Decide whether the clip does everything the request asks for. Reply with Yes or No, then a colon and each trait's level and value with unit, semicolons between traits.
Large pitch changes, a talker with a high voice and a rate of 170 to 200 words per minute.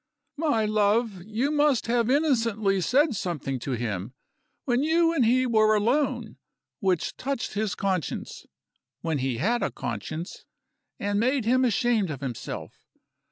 No: wide, 5.9 semitones; high, 220 Hz; average, 140 wpm